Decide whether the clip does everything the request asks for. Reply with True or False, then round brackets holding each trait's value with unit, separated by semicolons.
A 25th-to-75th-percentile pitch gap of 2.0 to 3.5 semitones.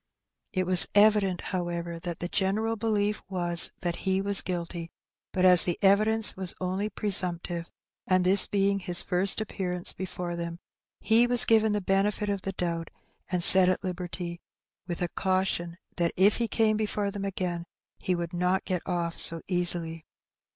True (2.5 semitones)